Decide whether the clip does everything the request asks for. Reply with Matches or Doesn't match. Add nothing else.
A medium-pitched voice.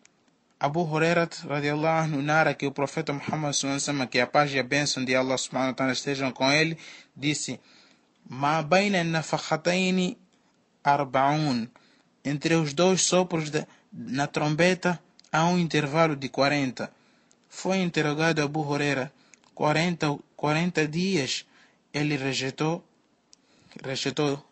Matches